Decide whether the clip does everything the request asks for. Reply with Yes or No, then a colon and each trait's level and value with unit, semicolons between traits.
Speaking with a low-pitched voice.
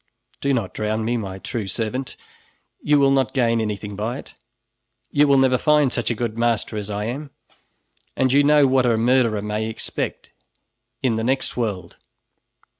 Yes: low, 120 Hz